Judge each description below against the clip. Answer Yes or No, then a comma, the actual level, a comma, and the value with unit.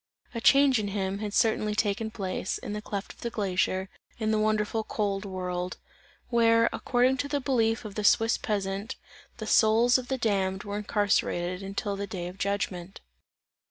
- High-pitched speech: Yes, high, 210 Hz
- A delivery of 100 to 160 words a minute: No, average, 175 wpm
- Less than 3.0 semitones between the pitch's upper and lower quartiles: Yes, narrow, 2.6 semitones